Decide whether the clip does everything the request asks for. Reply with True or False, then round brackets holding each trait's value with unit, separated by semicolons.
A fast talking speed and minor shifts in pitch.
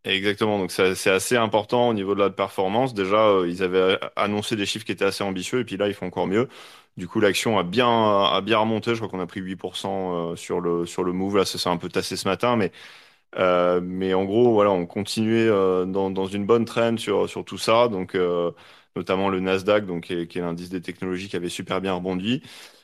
True (240 wpm; 2.3 semitones)